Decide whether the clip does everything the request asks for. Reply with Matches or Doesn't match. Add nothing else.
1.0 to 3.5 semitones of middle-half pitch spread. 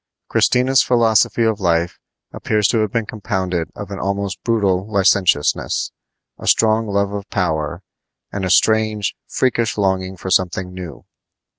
Matches